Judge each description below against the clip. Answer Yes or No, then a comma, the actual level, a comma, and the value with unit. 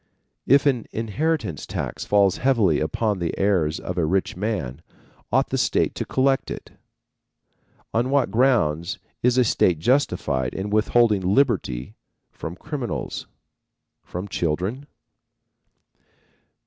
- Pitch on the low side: Yes, low, 105 Hz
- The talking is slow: Yes, slow, 120 wpm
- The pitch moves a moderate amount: No, wide, 6.5 semitones